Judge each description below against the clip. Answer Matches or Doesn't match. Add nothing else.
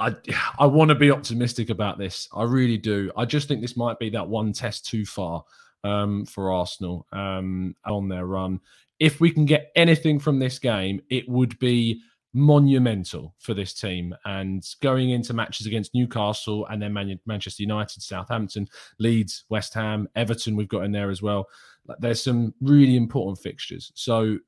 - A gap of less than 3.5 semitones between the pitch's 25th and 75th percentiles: Doesn't match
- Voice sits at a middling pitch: Doesn't match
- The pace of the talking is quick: Doesn't match